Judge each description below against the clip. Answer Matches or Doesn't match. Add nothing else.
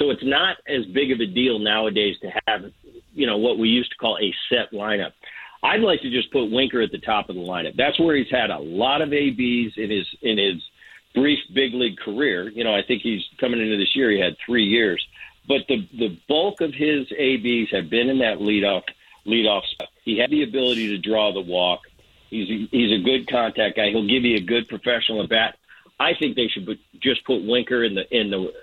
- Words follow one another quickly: Matches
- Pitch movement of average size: Matches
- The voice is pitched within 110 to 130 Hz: Matches